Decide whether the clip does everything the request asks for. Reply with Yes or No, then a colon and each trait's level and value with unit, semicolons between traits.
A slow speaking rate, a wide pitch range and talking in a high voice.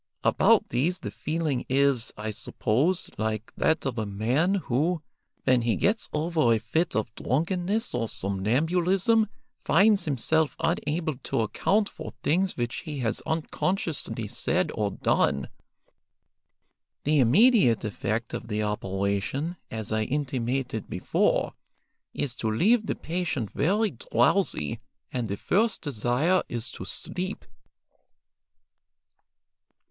No: slow, 120 wpm; wide, 7.7 semitones; low, 135 Hz